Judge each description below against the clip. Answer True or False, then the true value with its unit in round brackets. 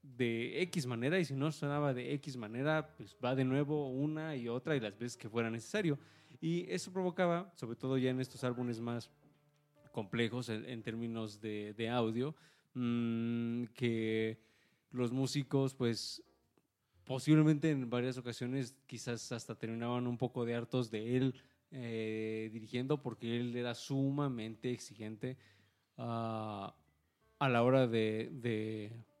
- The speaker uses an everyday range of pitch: True (3.2 semitones)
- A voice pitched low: True (125 Hz)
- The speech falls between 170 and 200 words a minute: False (145 wpm)